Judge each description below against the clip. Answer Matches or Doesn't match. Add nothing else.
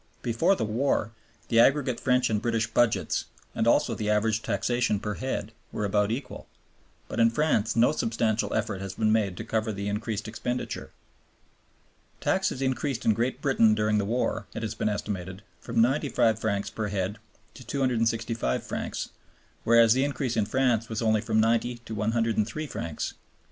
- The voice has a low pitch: Matches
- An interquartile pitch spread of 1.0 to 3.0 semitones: Matches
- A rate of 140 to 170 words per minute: Matches